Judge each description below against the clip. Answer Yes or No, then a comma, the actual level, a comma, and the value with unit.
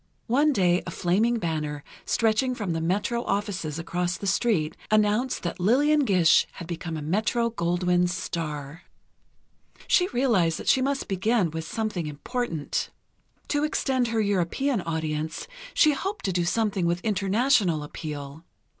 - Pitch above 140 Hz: Yes, high, 190 Hz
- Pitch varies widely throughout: Yes, wide, 6.0 semitones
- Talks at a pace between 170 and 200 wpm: No, average, 145 wpm